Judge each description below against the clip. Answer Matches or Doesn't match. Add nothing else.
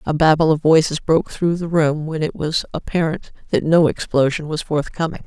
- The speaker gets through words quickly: Doesn't match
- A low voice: Doesn't match